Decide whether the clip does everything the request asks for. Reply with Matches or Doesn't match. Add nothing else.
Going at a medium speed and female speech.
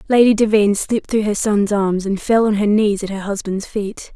Doesn't match